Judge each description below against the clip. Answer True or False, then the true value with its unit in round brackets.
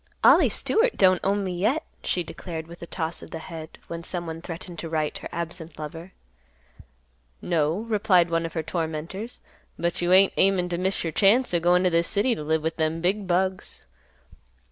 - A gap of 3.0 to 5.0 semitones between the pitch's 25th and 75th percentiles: False (2.6 semitones)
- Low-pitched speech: False (175 Hz)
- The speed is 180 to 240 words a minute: True (190 wpm)